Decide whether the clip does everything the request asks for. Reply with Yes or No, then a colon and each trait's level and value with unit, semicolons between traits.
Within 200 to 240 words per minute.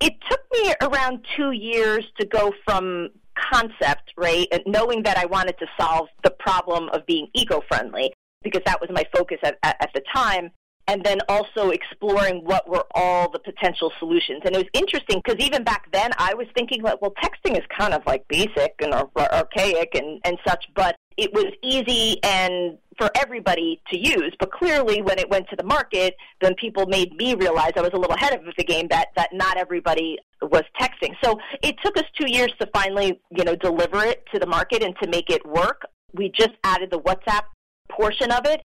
Yes: fast, 205 wpm